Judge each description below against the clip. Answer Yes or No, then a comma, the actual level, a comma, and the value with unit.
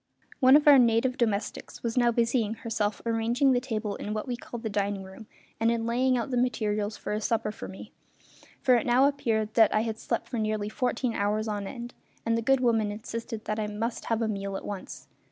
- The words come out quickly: Yes, fast, 225 wpm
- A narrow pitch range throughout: Yes, narrow, 2.3 semitones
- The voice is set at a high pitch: Yes, high, 225 Hz